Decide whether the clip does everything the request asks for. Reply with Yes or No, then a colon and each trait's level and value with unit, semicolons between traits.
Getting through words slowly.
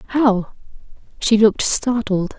Yes: slow, 100 wpm